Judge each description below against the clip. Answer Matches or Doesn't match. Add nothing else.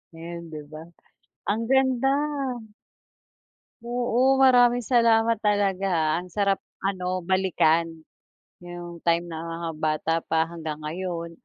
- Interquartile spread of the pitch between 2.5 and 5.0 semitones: Doesn't match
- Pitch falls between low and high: Matches